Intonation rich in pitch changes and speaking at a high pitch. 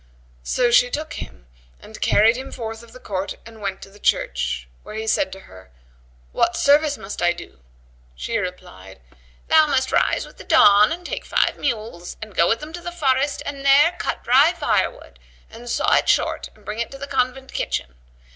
Yes: wide, 6.2 semitones; high, 235 Hz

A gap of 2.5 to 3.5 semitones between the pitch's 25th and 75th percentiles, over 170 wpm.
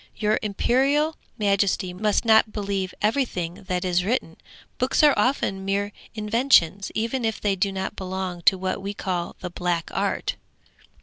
No: average, 3.2 semitones; average, 150 wpm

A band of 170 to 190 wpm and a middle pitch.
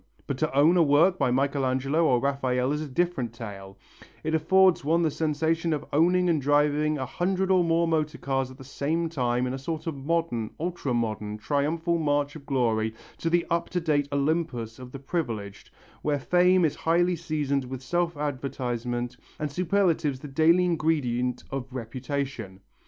Yes: average, 180 wpm; medium, 145 Hz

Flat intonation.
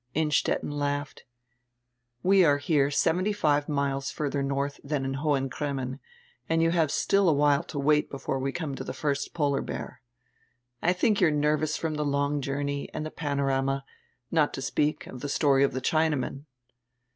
Yes: narrow, 1.9 semitones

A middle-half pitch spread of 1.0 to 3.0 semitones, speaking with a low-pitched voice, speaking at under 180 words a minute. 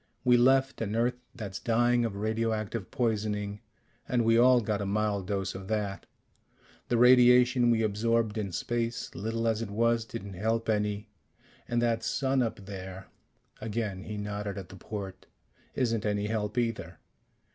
Yes: narrow, 2.5 semitones; low, 110 Hz; average, 160 wpm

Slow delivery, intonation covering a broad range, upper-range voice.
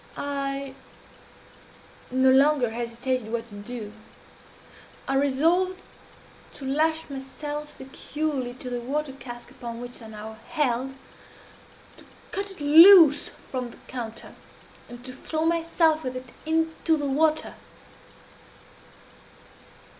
No: slow, 115 wpm; average, 4.1 semitones; very high, 270 Hz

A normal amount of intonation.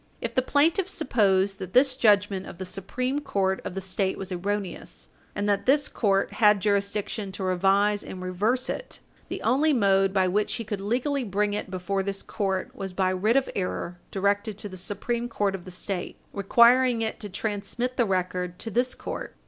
Yes: average, 3.6 semitones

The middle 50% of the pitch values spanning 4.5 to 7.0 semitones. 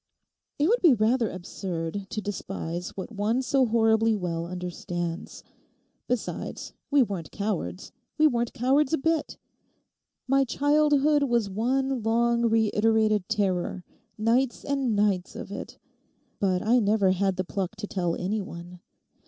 Yes: average, 5.1 semitones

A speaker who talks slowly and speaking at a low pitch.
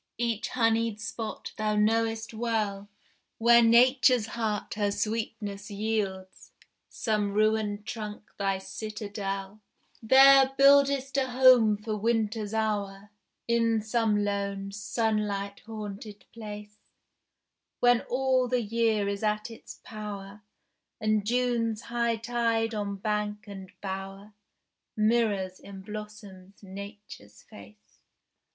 No: slow, 105 wpm; high, 215 Hz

